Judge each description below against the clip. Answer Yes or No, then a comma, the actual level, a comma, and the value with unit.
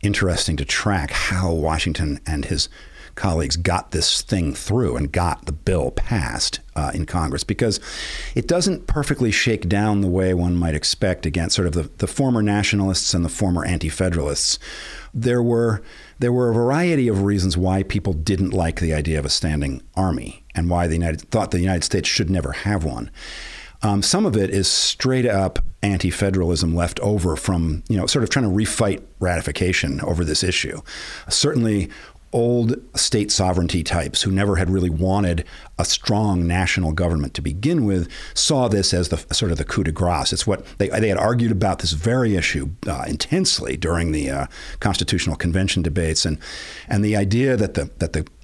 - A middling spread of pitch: Yes, average, 3.7 semitones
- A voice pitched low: Yes, very low, 95 Hz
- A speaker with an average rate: Yes, average, 180 wpm